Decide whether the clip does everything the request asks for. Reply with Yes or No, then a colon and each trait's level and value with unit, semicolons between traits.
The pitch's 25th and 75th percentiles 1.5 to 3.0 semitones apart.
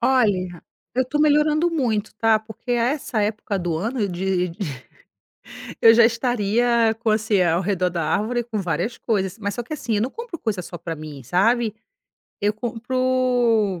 No: average, 4.2 semitones